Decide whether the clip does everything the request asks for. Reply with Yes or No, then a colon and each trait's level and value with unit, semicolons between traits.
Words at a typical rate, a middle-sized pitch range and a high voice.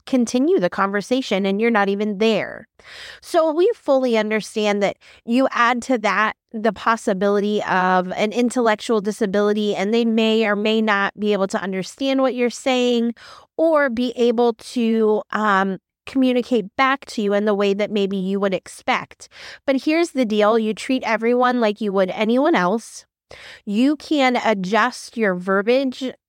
Yes: average, 160 wpm; average, 3.5 semitones; high, 225 Hz